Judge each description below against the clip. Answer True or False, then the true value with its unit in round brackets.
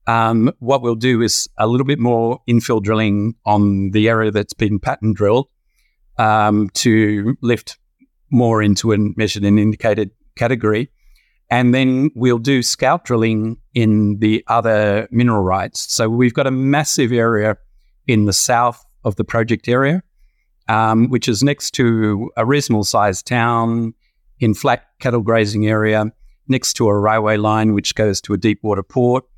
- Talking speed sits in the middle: True (160 wpm)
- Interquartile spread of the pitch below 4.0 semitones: True (2.4 semitones)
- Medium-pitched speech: False (115 Hz)